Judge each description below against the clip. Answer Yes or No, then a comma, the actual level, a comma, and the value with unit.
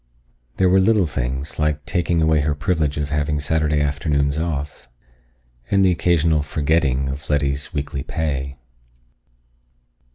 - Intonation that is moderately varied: No, narrow, 2.0 semitones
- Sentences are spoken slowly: Yes, slow, 130 wpm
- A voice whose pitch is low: Yes, very low, 75 Hz